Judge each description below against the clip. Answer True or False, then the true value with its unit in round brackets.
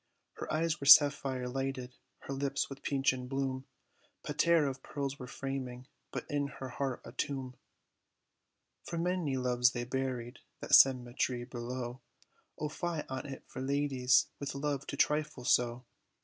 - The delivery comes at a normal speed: True (150 wpm)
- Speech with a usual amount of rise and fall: False (2.0 semitones)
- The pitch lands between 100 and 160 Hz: True (135 Hz)